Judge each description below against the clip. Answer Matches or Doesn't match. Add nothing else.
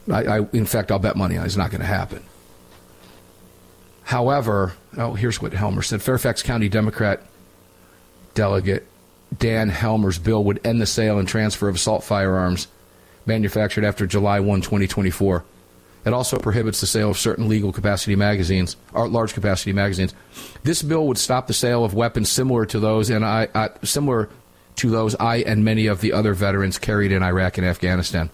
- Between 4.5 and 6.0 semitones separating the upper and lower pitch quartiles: Doesn't match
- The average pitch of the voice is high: Doesn't match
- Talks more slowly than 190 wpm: Matches